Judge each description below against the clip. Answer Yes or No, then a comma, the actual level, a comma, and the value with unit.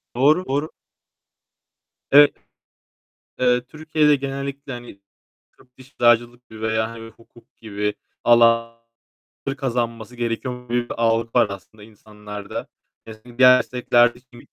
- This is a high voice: No, low, 120 Hz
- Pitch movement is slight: Yes, narrow, 2.1 semitones